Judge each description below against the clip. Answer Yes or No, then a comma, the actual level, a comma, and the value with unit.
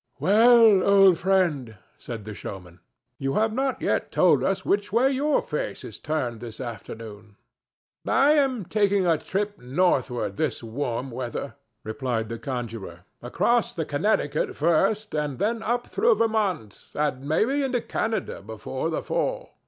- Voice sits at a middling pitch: Yes, medium, 155 Hz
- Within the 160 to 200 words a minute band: No, average, 145 wpm